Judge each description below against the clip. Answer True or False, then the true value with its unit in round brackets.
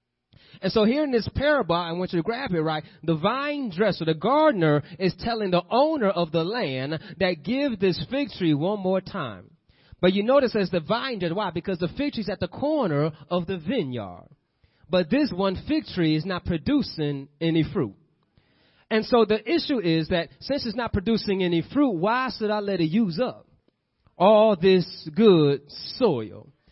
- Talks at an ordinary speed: True (190 wpm)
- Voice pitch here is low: False (190 Hz)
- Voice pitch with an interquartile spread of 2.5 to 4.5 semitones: False (5.6 semitones)